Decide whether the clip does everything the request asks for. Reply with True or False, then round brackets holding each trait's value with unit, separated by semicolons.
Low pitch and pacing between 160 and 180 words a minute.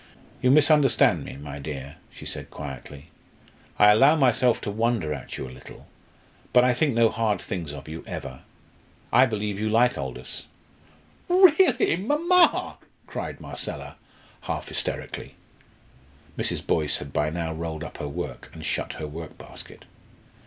False (105 Hz; 145 wpm)